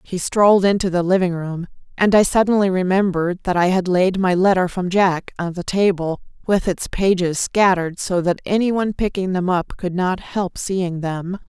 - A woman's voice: Yes, female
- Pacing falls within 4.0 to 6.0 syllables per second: Yes, 5.0 syllables/s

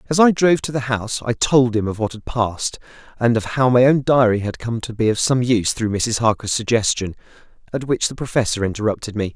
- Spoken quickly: Yes, fast, 230 wpm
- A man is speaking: Yes, male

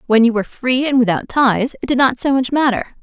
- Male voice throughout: No, female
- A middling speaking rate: No, fast, 260 wpm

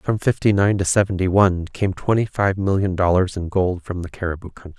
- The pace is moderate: No, fast, 215 wpm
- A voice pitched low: Yes, very low, 95 Hz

